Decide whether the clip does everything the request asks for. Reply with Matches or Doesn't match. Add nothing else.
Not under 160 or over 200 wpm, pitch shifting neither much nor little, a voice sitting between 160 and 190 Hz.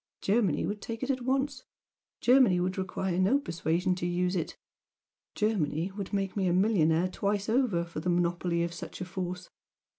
Matches